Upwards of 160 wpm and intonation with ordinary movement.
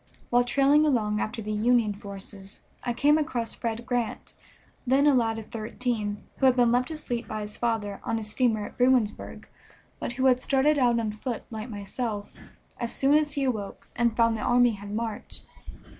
Yes: average, 190 wpm; average, 3.0 semitones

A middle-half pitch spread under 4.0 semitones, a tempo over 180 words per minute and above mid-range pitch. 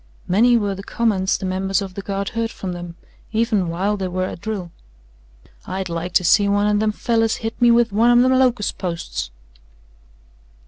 Yes: average, 3.4 semitones; average, 190 wpm; high, 200 Hz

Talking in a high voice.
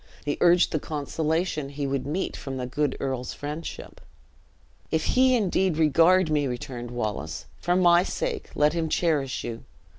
No: medium, 150 Hz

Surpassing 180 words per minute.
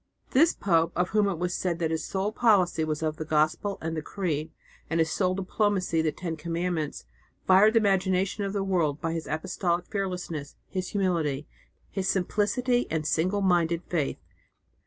No: average, 170 wpm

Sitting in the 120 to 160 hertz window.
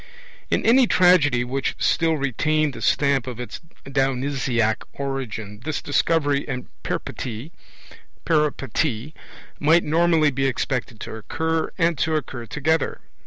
Yes: medium, 140 Hz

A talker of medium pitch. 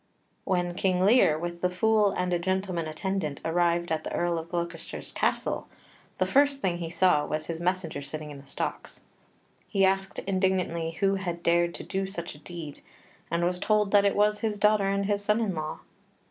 Yes: medium, 180 Hz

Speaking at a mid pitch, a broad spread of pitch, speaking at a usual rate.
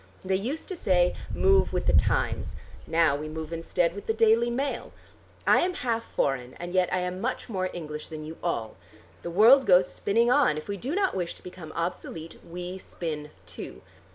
Yes: medium, 180 Hz; wide, 5.7 semitones; average, 195 wpm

